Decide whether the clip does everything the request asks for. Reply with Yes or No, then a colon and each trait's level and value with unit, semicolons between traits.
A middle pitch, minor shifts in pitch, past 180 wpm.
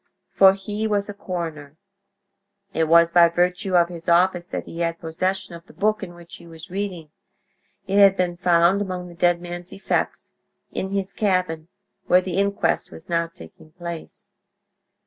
No: medium, 175 Hz; narrow, 2.2 semitones; average, 165 wpm